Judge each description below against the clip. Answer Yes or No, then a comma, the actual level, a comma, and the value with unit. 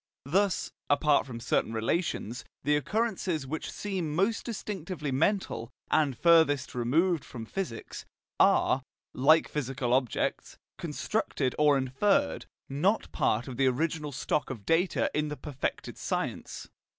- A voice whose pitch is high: No, medium, 150 Hz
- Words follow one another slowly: Yes, slow, 125 wpm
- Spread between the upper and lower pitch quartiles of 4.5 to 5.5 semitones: Yes, average, 5.2 semitones